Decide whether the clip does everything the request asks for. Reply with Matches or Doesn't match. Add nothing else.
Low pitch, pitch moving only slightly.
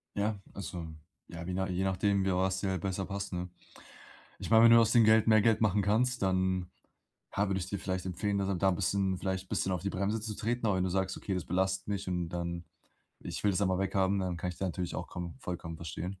Matches